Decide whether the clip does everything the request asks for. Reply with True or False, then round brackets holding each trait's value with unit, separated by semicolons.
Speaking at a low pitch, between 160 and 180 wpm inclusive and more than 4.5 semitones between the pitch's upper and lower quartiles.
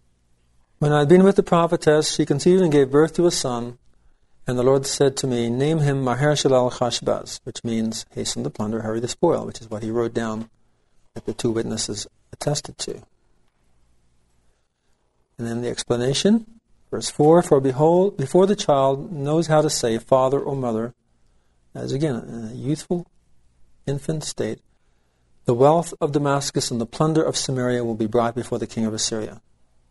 True (125 Hz; 175 wpm; 5.4 semitones)